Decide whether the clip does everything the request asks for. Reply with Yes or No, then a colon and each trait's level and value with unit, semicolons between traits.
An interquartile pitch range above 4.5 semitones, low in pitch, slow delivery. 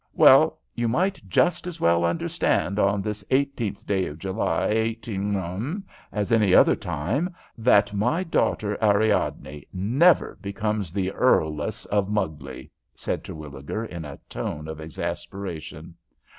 Yes: average, 4.9 semitones; low, 100 Hz; slow, 130 wpm